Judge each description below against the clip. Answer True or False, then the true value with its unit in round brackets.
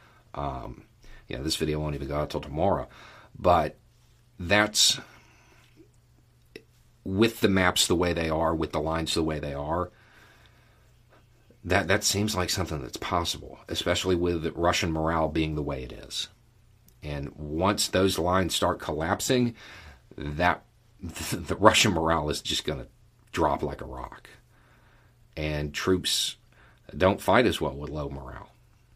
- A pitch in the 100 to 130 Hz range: False (90 Hz)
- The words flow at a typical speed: True (145 wpm)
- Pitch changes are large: True (5.9 semitones)